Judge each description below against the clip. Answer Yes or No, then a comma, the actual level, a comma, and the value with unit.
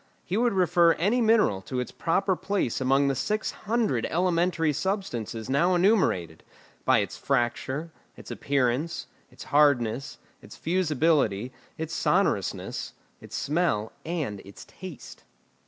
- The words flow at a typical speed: No, slow, 125 wpm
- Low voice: No, medium, 155 Hz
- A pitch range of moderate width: No, wide, 6.2 semitones